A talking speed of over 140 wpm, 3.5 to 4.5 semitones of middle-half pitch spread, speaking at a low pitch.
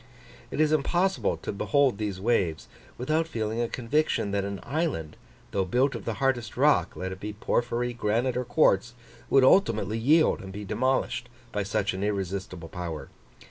No: average, 170 wpm; average, 5.1 semitones; low, 115 Hz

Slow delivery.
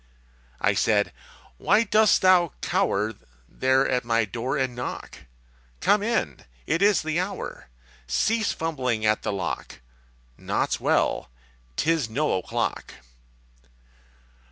Yes: slow, 115 wpm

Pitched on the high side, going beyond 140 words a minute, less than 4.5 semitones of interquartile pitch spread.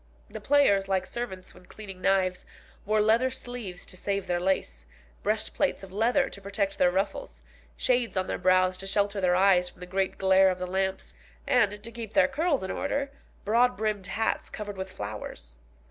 Yes: high, 195 Hz; average, 185 wpm; average, 3.4 semitones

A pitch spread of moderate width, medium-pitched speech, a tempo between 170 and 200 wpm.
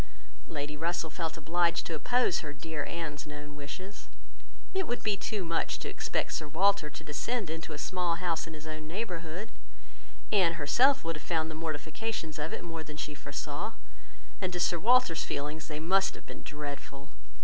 Yes: average, 3.2 semitones; medium, 165 Hz; average, 180 wpm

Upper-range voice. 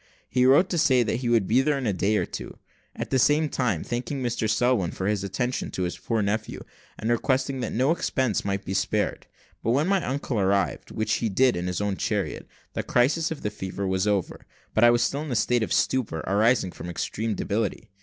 No: low, 115 Hz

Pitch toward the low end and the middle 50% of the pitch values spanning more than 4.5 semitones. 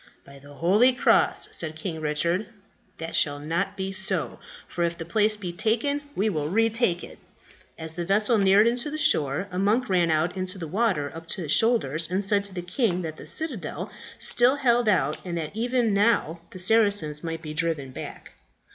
No: medium, 185 Hz; average, 5.1 semitones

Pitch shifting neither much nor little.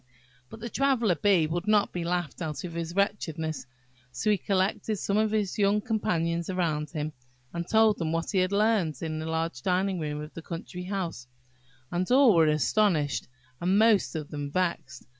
Yes: average, 4.2 semitones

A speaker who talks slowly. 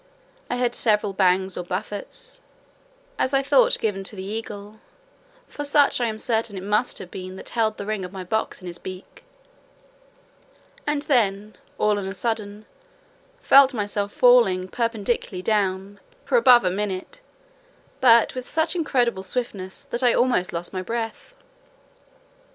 No: average, 155 wpm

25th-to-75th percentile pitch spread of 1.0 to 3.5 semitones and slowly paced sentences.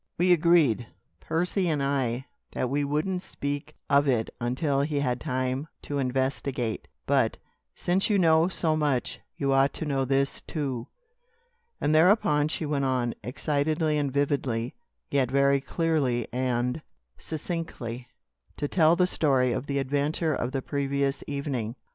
No: average, 3.2 semitones; average, 145 wpm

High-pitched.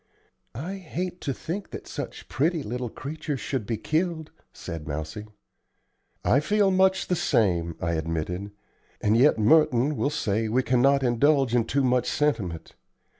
No: low, 130 Hz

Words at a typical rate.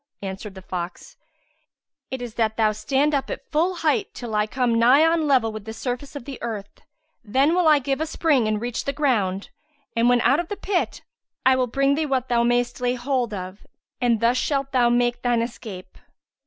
No: fast, 210 wpm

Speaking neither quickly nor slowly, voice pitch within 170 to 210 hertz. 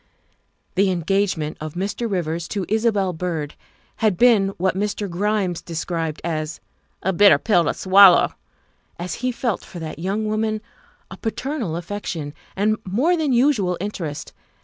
Yes: average, 150 wpm; high, 190 Hz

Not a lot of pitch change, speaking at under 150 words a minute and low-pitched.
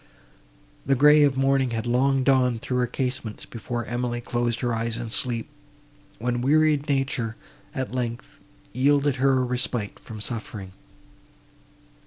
Yes: narrow, 2.3 semitones; average, 140 wpm; low, 125 Hz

